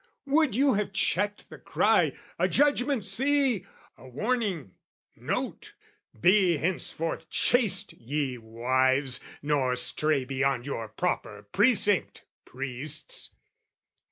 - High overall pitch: No, medium, 155 Hz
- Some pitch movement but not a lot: No, wide, 8.3 semitones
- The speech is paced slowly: Yes, slow, 100 wpm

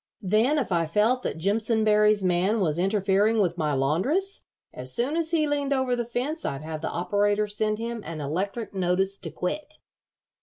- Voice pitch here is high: Yes, high, 210 Hz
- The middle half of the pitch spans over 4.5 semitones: Yes, average, 5.2 semitones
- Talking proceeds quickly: No, average, 180 wpm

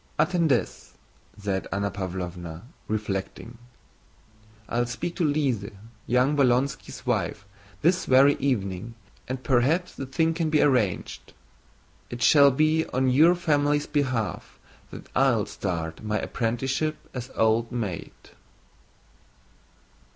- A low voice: Yes, low, 125 Hz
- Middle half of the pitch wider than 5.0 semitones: Yes, wide, 5.5 semitones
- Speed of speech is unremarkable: No, slow, 110 wpm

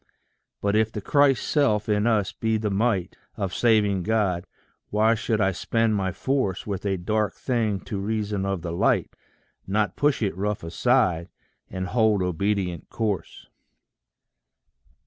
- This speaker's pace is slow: No, average, 145 wpm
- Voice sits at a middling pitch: No, low, 105 Hz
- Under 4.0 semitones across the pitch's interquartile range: Yes, narrow, 2.6 semitones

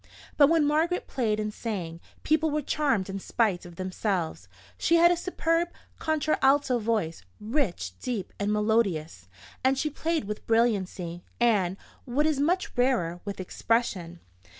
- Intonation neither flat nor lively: No, wide, 7.8 semitones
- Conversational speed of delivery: Yes, average, 145 wpm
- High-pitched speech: Yes, high, 230 Hz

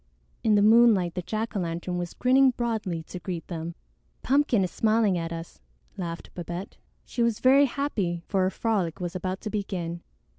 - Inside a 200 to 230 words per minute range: No, average, 180 wpm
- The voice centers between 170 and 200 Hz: Yes, high, 190 Hz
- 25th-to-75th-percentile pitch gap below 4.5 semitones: No, average, 4.8 semitones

